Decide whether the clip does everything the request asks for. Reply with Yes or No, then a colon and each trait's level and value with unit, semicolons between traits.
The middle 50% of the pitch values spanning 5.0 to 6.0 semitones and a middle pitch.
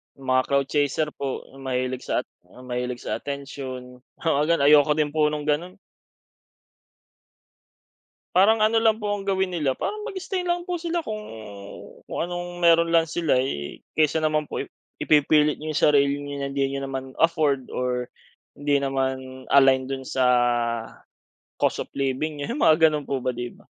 No: average, 4.0 semitones; medium, 145 Hz